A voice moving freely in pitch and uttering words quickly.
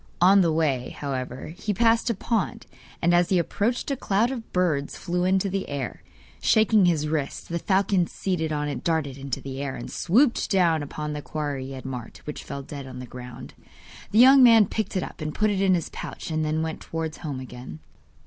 Yes: wide, 5.7 semitones; fast, 215 wpm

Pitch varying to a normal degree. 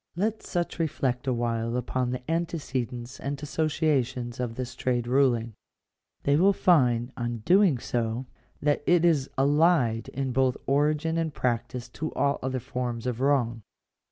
Yes: average, 4.1 semitones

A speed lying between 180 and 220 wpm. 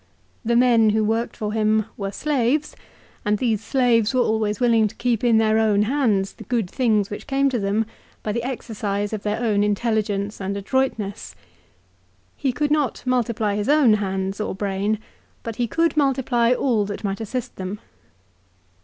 No: average, 170 wpm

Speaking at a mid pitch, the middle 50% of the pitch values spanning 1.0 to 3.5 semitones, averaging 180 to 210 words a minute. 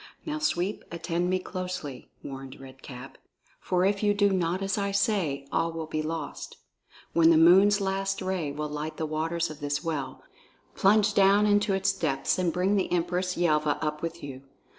No: medium, 170 Hz; average, 4.0 semitones; average, 185 wpm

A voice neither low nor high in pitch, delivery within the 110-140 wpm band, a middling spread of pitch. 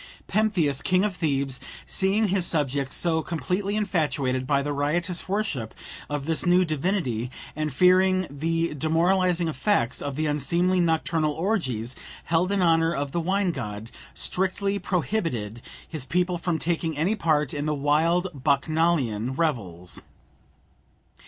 Yes: medium, 160 Hz; slow, 135 wpm; average, 4.5 semitones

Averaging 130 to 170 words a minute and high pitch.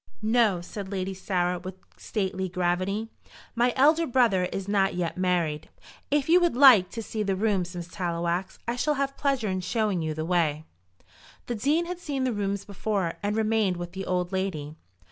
No: average, 185 wpm; high, 195 Hz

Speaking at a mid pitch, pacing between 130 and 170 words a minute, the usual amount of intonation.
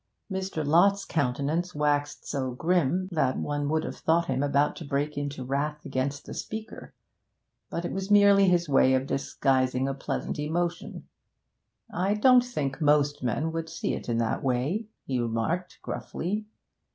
Yes: medium, 150 Hz; average, 160 wpm; average, 4.5 semitones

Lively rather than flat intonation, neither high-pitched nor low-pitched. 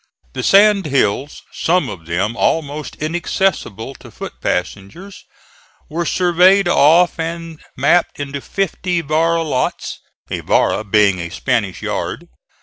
Yes: wide, 7.2 semitones; medium, 155 Hz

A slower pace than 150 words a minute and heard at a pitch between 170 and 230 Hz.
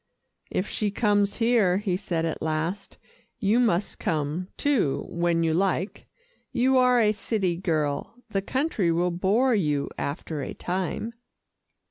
Yes: average, 140 wpm; high, 190 Hz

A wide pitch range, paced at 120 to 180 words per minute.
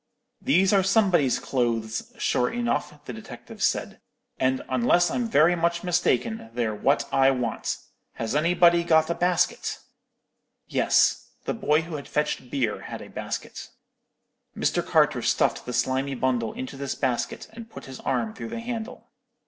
Yes: wide, 5.9 semitones; average, 155 wpm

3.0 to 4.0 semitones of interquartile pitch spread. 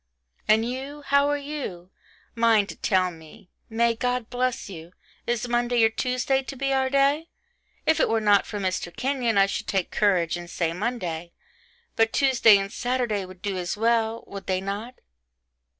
No: average, 4.7 semitones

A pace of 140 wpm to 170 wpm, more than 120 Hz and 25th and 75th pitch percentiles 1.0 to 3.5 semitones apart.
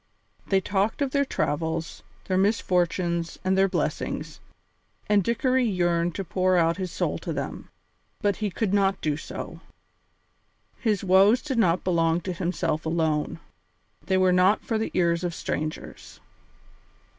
Yes: average, 145 wpm; medium, 185 Hz; average, 3.2 semitones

